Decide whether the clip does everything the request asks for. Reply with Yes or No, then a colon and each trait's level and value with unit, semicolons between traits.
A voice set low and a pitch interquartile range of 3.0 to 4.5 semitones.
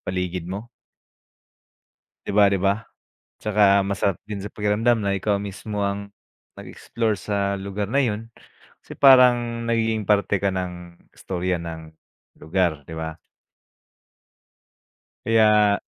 No: low, 100 Hz; narrow, 2.4 semitones